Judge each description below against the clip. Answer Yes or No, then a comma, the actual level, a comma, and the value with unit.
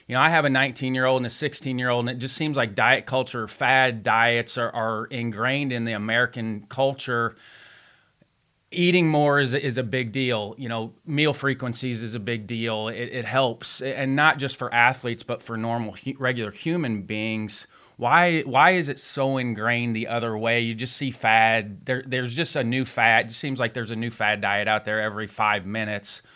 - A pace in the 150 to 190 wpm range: No, average, 200 wpm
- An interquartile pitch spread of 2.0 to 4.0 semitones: Yes, average, 3.0 semitones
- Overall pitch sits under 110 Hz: No, low, 120 Hz